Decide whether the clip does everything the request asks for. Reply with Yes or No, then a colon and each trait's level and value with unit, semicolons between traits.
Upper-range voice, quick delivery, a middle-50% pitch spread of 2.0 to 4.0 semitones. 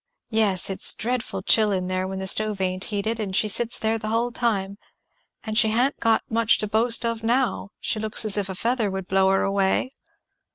Yes: high, 215 Hz; fast, 210 wpm; average, 2.9 semitones